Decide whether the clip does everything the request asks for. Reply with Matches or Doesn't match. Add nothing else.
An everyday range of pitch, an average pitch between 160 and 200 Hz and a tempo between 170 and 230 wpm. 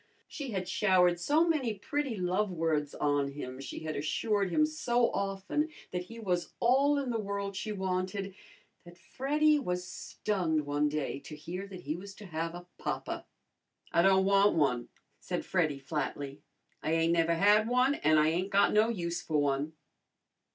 Matches